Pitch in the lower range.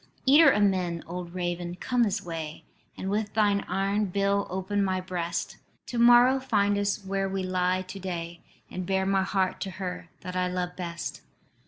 No: high, 190 Hz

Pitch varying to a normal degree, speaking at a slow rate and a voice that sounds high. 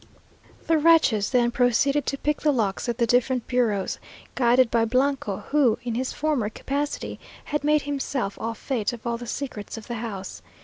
No: average, 3.7 semitones; average, 180 wpm; high, 245 Hz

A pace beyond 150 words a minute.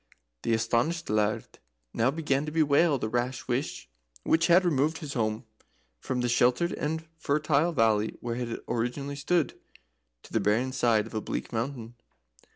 Yes: average, 160 wpm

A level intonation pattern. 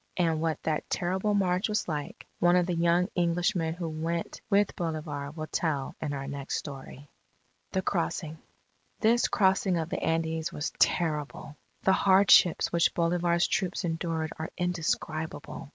Yes: narrow, 2.2 semitones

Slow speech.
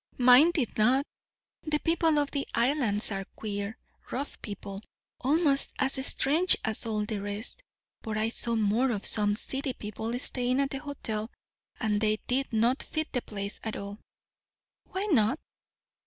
No: average, 155 wpm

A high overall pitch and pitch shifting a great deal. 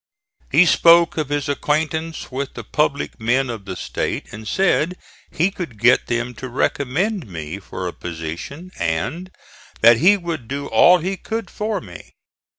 No: medium, 140 Hz; wide, 7.4 semitones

